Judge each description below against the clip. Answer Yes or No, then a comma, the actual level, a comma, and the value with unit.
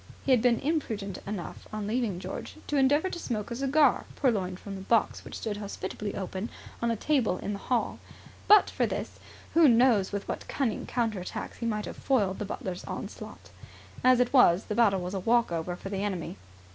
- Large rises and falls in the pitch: No, average, 4.4 semitones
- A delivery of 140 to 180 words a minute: No, fast, 205 wpm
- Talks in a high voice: Yes, high, 215 Hz